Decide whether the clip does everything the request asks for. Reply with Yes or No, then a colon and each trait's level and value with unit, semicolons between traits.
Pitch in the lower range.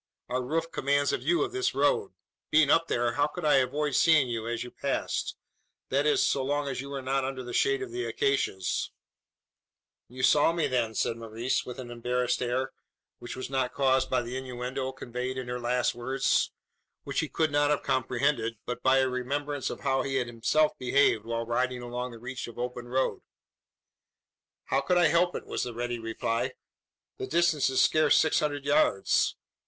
Yes: low, 130 Hz